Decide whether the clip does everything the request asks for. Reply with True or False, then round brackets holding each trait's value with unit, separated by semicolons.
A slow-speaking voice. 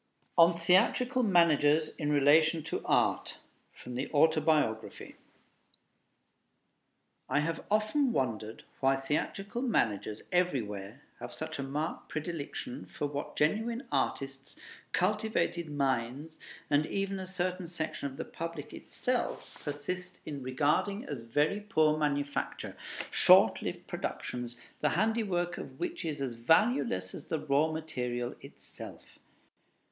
True (120 wpm)